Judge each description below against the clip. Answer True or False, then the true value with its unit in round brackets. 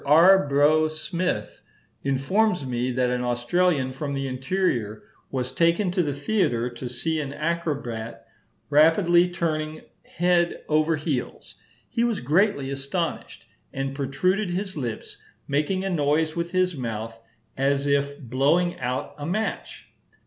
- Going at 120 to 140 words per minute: True (135 wpm)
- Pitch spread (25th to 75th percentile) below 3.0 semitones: False (4.7 semitones)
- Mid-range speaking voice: True (150 Hz)